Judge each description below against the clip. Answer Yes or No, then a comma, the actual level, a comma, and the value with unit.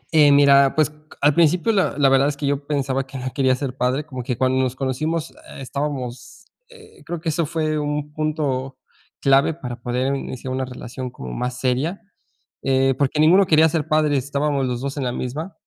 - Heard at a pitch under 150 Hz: Yes, medium, 140 Hz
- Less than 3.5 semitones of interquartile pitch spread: Yes, average, 2.9 semitones